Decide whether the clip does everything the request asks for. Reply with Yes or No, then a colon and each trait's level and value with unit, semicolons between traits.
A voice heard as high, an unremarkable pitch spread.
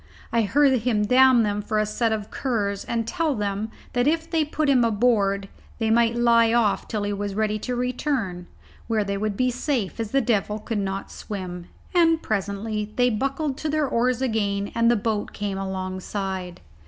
Yes: high, 220 Hz; average, 3.7 semitones